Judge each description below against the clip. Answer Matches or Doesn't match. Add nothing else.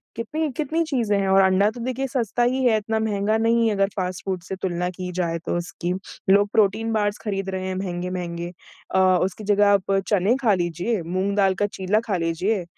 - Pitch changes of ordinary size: Matches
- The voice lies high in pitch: Matches